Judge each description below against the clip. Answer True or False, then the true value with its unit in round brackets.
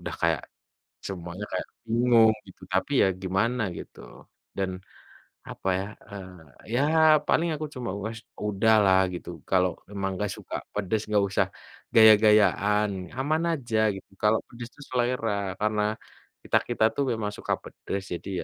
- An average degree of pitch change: True (3.2 semitones)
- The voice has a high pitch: False (105 Hz)